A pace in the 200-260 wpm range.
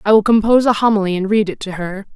No: fast, 280 wpm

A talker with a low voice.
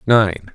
Yes: low, 100 Hz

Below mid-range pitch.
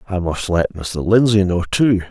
Yes: very low, 95 Hz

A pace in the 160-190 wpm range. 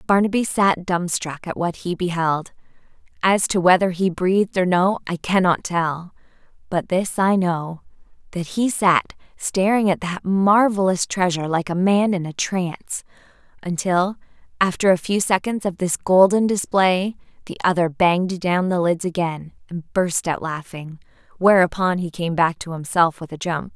Yes: average, 165 wpm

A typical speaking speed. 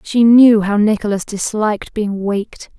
Yes: average, 150 wpm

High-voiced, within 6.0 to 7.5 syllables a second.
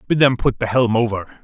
No: low, 120 Hz; 6.2 syllables/s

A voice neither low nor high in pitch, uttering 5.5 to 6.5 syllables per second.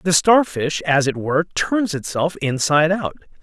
No: medium, 165 Hz; 4.7 syllables/s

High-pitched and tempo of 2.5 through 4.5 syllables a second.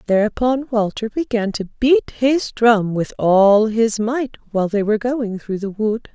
Yes: high, 225 Hz; 4.2 syllables/s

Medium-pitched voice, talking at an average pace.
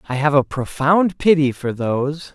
Yes: medium, 145 Hz; average, 180 wpm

